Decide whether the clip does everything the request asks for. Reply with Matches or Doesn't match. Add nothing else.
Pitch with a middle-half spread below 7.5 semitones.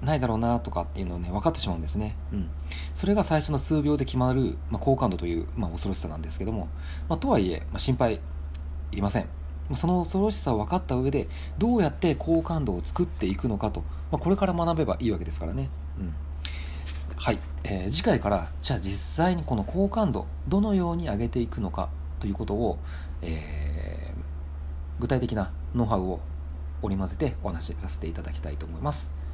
Doesn't match